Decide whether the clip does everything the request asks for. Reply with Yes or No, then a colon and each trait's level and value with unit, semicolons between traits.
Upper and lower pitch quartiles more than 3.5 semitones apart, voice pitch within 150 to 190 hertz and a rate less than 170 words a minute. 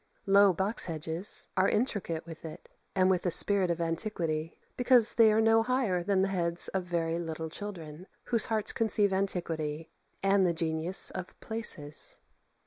Yes: average, 3.9 semitones; medium, 185 Hz; average, 160 wpm